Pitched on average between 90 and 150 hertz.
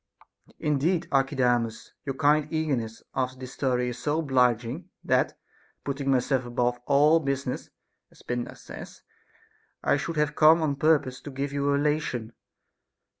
Yes: medium, 140 Hz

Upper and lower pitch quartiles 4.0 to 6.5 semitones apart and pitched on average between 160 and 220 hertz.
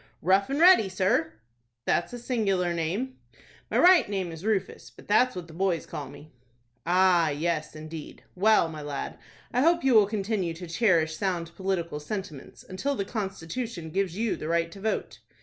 Yes: average, 4.7 semitones; medium, 185 Hz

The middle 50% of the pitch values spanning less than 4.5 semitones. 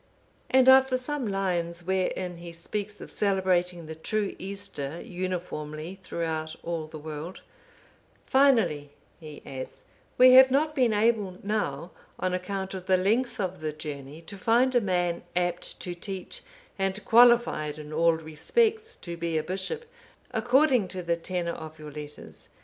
No: average, 5.0 semitones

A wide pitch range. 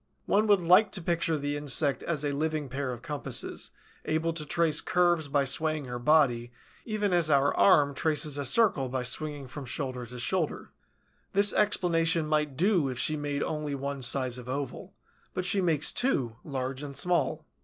No: average, 3.6 semitones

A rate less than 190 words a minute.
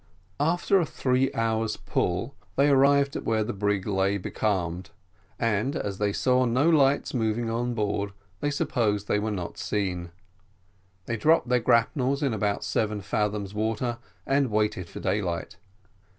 Yes: average, 150 wpm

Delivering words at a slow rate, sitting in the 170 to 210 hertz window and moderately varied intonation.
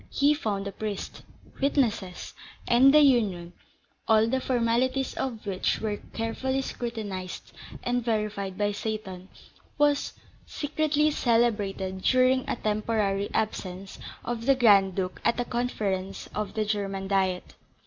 No: slow, 130 wpm; high, 220 Hz; average, 4.1 semitones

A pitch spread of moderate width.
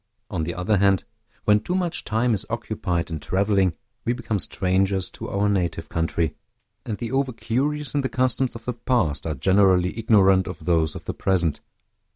Yes: average, 4.6 semitones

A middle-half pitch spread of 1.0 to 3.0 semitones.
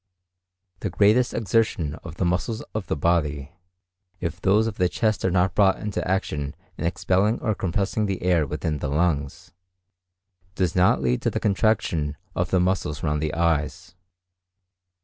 No: average, 4.7 semitones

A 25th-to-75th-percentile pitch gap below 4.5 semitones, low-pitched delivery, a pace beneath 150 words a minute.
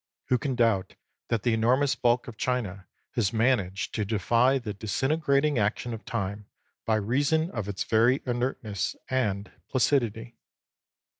Yes: average, 3.6 semitones; low, 115 Hz; average, 140 wpm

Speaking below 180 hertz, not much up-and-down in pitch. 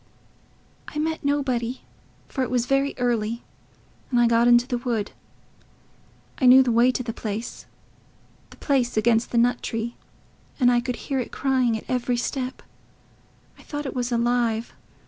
No: high, 245 Hz; narrow, 1.8 semitones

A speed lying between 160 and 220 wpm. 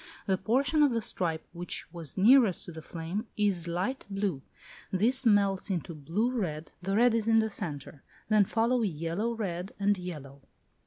Yes: average, 170 wpm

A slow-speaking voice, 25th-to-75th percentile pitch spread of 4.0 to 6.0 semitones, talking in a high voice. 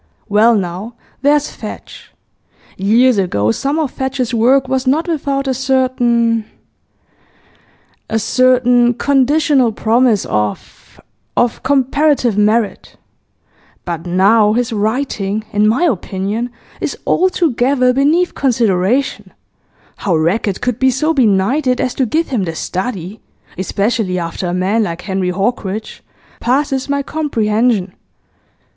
Yes: slow, 115 wpm; average, 4.7 semitones; high, 235 Hz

